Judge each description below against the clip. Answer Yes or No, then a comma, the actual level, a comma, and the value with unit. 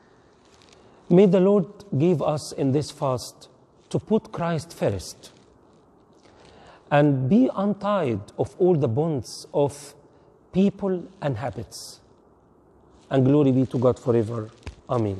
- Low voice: No, medium, 145 Hz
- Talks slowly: Yes, slow, 120 wpm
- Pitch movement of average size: No, wide, 6.5 semitones